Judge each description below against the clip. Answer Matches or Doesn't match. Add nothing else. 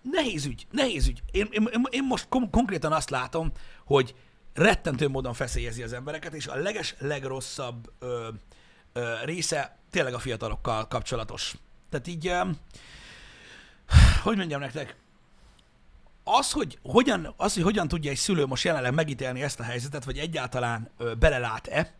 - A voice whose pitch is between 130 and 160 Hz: Matches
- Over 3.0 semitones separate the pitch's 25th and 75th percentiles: Matches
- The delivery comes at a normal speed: Matches